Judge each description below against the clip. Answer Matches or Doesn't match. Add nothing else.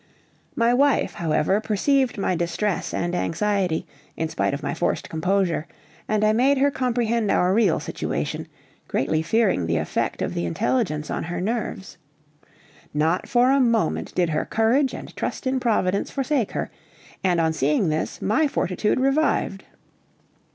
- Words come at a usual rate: Matches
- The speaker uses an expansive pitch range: Matches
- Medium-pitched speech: Doesn't match